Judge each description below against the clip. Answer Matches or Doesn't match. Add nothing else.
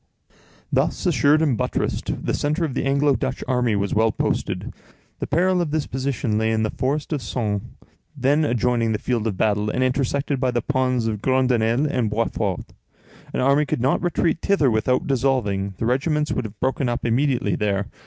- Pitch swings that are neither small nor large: Matches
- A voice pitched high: Doesn't match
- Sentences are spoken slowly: Doesn't match